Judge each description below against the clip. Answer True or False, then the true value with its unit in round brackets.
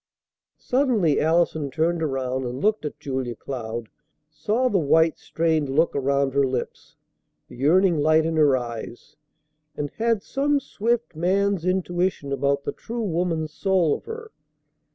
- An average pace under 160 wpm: True (145 wpm)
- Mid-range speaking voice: True (160 Hz)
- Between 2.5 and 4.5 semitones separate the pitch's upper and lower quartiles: False (5.6 semitones)